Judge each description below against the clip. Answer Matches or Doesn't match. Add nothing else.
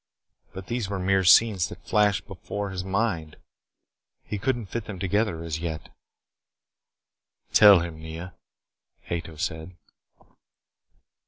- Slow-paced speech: Matches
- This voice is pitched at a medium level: Doesn't match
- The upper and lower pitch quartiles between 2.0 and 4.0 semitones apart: Matches